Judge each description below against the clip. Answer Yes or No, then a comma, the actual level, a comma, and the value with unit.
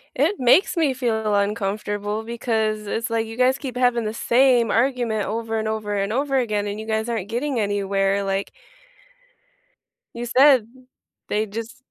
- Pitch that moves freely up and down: No, average, 2.9 semitones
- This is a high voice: Yes, high, 225 Hz